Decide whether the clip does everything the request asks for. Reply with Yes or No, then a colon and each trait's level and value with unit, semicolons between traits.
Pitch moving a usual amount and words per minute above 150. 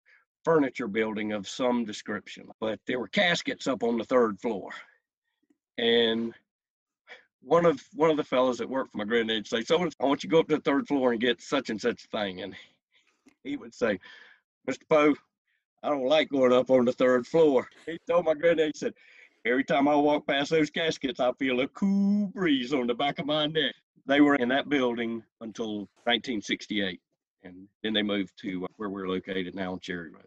No: wide, 6.0 semitones; average, 200 wpm